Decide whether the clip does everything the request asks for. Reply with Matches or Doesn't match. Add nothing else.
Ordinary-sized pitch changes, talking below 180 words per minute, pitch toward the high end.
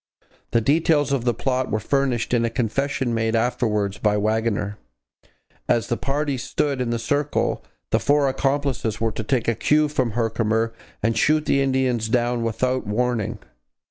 Doesn't match